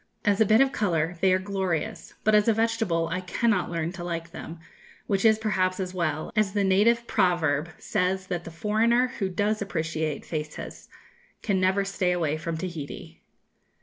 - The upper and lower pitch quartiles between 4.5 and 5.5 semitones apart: No, average, 3.9 semitones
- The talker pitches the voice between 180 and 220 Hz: Yes, medium, 185 Hz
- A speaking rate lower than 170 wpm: No, average, 180 wpm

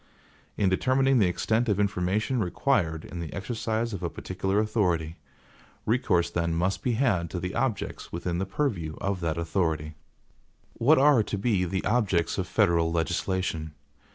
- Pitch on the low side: Yes, very low, 95 Hz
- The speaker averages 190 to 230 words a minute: No, average, 155 wpm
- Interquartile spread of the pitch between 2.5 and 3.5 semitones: No, average, 4.7 semitones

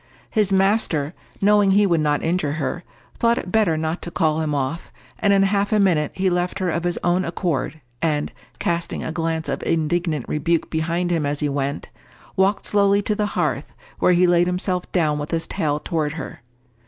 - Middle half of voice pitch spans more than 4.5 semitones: No, average, 3.5 semitones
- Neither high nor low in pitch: Yes, medium, 170 Hz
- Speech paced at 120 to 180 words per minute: No, average, 195 wpm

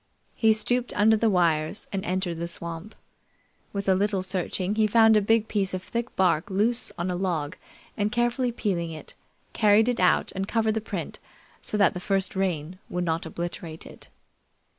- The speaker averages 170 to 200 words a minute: Yes, average, 185 wpm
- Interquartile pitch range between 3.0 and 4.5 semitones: Yes, average, 3.8 semitones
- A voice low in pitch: No, high, 195 Hz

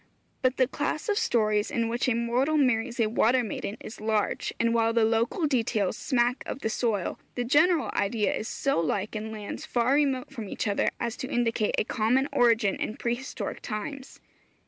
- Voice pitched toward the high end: Yes, high, 235 Hz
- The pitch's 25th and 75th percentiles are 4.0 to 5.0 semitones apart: No, average, 2.9 semitones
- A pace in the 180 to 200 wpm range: Yes, average, 190 wpm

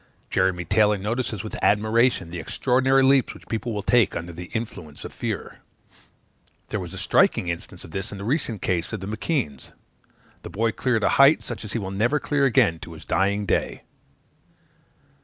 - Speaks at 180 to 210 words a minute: Yes, average, 185 wpm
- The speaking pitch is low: Yes, low, 105 Hz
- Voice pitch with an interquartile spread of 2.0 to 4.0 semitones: No, average, 4.7 semitones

